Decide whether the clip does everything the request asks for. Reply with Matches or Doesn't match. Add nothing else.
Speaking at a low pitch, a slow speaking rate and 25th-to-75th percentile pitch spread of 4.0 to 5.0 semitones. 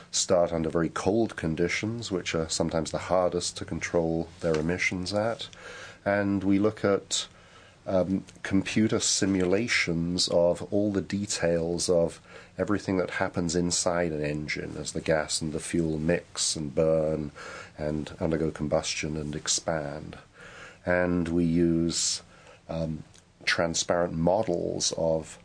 Doesn't match